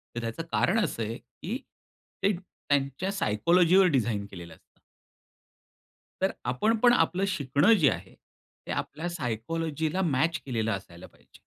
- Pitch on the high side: No, medium, 150 Hz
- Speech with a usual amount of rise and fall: No, wide, 7.9 semitones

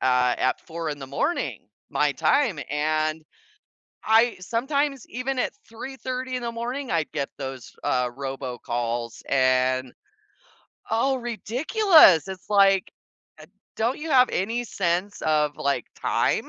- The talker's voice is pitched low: No, high, 190 Hz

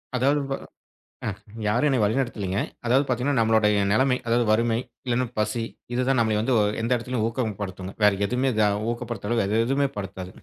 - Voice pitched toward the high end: No, low, 115 Hz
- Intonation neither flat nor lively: Yes, average, 3.2 semitones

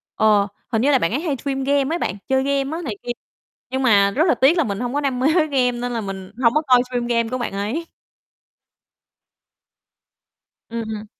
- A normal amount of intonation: Yes, average, 3.9 semitones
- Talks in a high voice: Yes, very high, 250 Hz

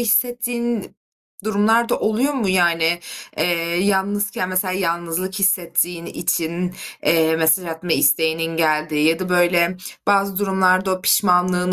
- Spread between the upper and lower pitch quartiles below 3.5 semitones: Yes, average, 3.0 semitones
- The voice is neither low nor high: Yes, medium, 180 Hz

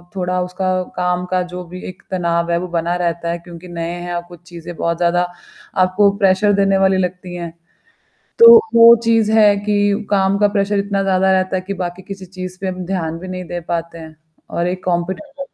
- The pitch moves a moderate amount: No, narrow, 2.1 semitones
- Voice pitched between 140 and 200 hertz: Yes, medium, 185 Hz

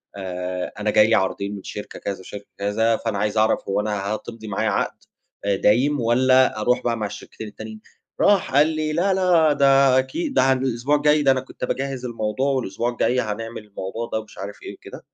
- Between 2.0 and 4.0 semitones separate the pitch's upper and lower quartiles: No, average, 4.4 semitones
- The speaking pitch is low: Yes, low, 115 Hz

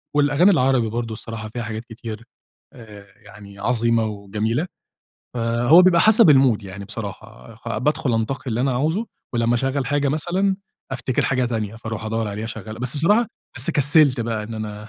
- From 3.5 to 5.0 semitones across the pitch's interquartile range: Yes, average, 4.0 semitones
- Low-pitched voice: Yes, low, 115 Hz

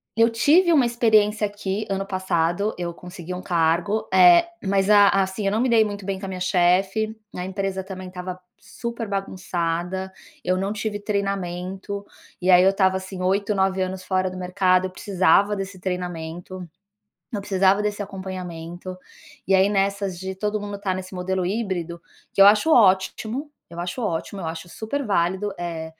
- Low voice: No, high, 190 Hz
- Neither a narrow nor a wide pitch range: No, narrow, 2.1 semitones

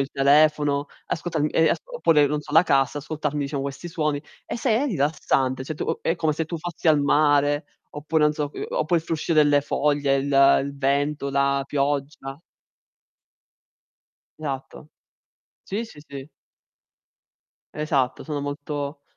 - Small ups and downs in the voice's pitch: Yes, narrow, 1.8 semitones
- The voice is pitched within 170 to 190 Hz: No, medium, 145 Hz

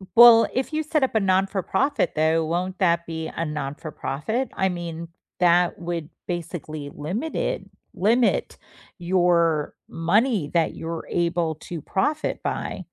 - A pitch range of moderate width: Yes, average, 3.2 semitones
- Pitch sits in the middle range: Yes, medium, 175 Hz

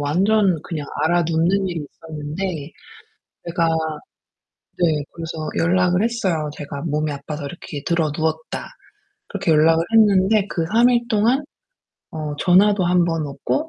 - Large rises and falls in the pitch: No, average, 3.9 semitones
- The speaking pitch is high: No, medium, 170 Hz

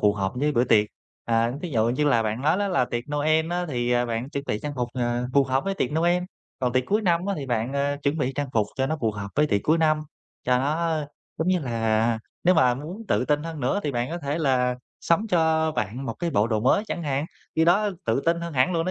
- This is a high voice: No, medium, 140 Hz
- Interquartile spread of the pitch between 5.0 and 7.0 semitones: Yes, average, 5.3 semitones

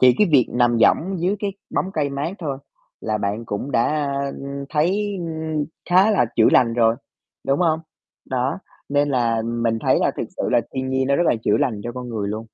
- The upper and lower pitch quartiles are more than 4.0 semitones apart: Yes, average, 4.7 semitones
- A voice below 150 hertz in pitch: Yes, low, 135 Hz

